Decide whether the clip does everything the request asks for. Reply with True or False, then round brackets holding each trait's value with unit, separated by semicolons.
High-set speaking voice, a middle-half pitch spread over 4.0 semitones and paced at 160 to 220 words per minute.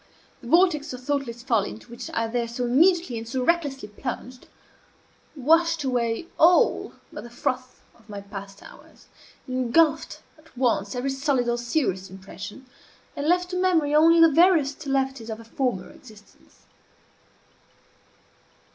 False (255 Hz; 4.9 semitones; 145 wpm)